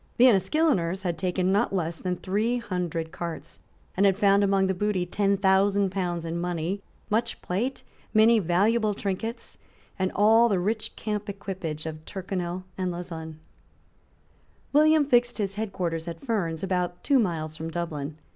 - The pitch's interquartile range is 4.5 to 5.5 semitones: No, average, 3.4 semitones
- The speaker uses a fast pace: No, average, 155 wpm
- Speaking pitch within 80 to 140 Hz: No, high, 190 Hz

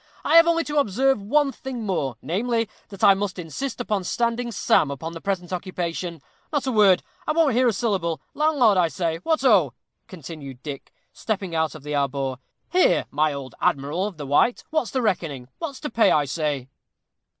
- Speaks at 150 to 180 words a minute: No, average, 190 wpm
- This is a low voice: No, high, 190 Hz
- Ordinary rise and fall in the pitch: No, wide, 7.8 semitones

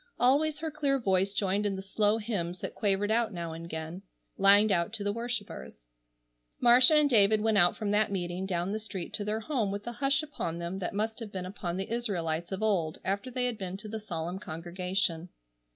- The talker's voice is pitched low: No, high, 200 Hz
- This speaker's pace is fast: Yes, fast, 215 wpm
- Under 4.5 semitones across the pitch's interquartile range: Yes, average, 3.7 semitones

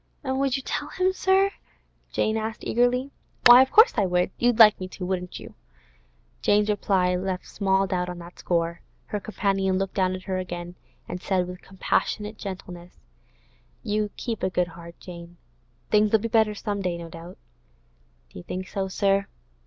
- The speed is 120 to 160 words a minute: No, average, 175 wpm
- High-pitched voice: Yes, high, 195 Hz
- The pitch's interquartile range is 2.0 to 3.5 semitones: Yes, average, 3.2 semitones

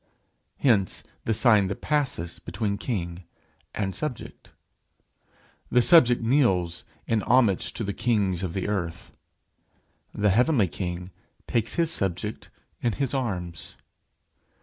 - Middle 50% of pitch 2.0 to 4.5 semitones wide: No, average, 5.0 semitones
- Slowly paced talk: Yes, slow, 120 wpm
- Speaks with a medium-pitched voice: No, low, 105 Hz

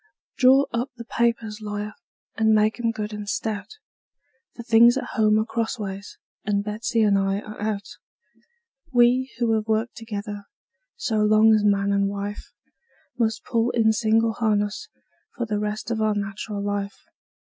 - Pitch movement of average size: No, narrow, 1.7 semitones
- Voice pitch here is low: No, high, 215 Hz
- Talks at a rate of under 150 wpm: No, average, 160 wpm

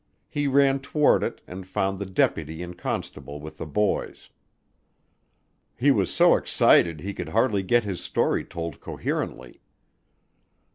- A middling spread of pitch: No, wide, 6.3 semitones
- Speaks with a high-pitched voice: No, very low, 95 Hz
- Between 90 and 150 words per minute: Yes, average, 140 wpm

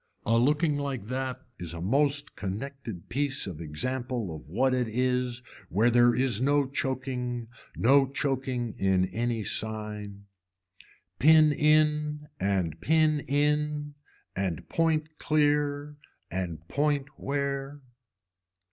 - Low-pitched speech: Yes, low, 130 Hz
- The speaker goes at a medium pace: No, slow, 115 wpm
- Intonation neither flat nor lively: Yes, average, 5.0 semitones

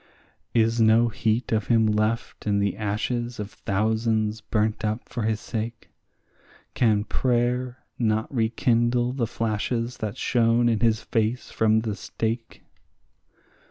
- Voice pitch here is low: Yes, low, 115 Hz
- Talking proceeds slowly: Yes, slow, 130 wpm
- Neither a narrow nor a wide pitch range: No, narrow, 1.6 semitones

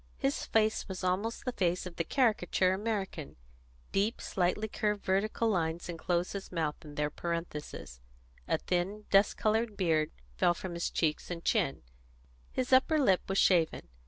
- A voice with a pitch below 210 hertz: Yes, medium, 185 Hz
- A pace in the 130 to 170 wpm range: Yes, average, 160 wpm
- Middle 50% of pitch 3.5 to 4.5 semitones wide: Yes, average, 4.0 semitones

